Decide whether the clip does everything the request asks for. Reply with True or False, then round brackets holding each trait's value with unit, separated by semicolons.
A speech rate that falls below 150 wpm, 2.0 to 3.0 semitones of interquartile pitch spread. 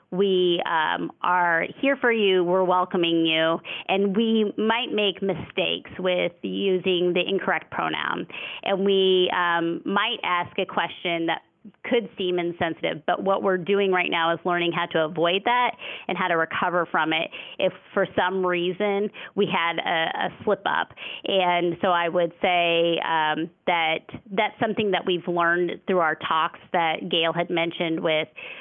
False (165 wpm; 2.4 semitones)